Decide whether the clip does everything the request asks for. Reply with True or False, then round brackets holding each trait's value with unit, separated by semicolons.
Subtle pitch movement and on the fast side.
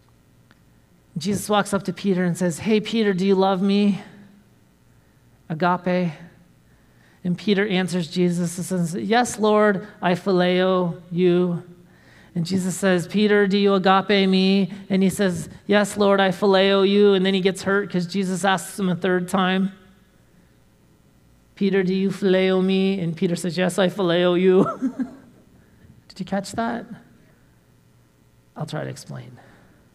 False (1.9 semitones; 145 wpm)